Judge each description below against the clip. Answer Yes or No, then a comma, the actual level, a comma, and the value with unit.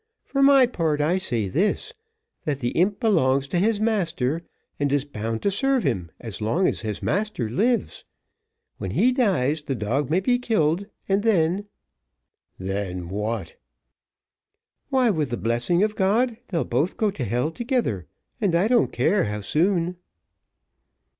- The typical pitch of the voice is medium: Yes, medium, 165 Hz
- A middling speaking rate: Yes, average, 160 wpm